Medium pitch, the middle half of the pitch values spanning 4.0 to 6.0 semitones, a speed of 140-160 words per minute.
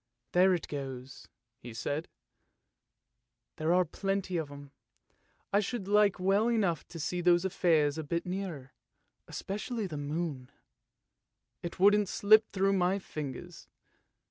Yes: medium, 175 Hz; average, 5.1 semitones; average, 145 wpm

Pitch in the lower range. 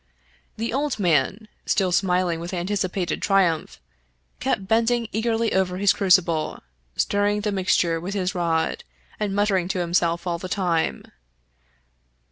No: medium, 185 Hz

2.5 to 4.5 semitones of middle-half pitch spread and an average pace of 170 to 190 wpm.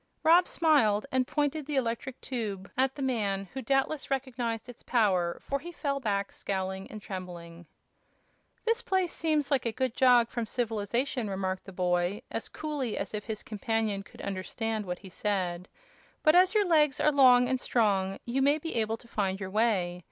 No: wide, 5.5 semitones; average, 180 wpm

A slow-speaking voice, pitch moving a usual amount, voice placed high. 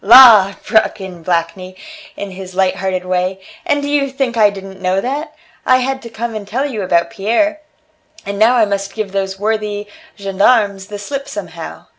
No: average, 185 wpm; average, 3.9 semitones; high, 205 Hz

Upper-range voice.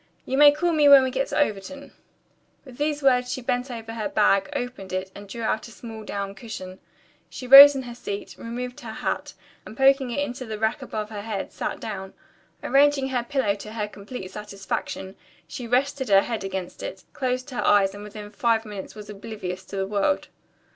Yes: high, 225 Hz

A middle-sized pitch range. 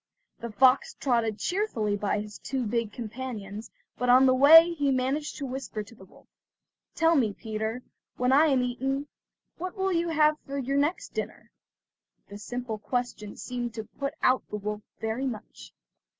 Yes: average, 4.2 semitones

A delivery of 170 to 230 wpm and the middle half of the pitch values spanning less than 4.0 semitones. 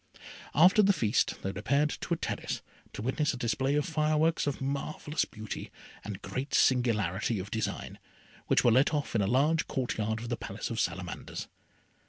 No: average, 180 wpm; wide, 5.5 semitones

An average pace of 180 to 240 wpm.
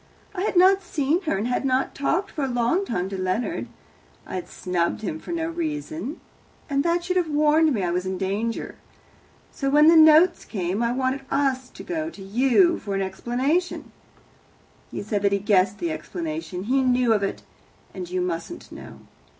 Yes: average, 190 wpm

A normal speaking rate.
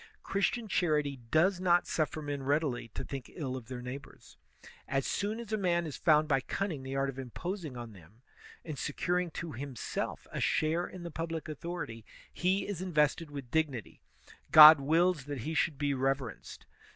Yes: average, 175 wpm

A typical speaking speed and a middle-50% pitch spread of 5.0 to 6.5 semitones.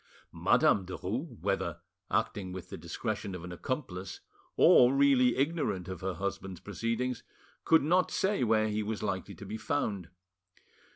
Yes: average, 150 wpm; average, 5.3 semitones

